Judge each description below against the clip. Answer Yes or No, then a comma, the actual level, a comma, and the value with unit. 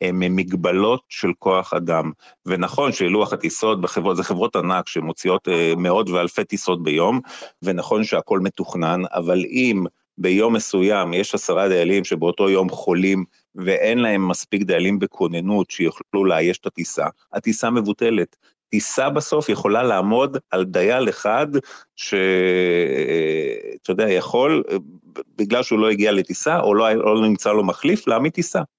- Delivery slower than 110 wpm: No, average, 135 wpm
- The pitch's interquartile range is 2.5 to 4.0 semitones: No, wide, 5.4 semitones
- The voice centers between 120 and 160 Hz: No, low, 100 Hz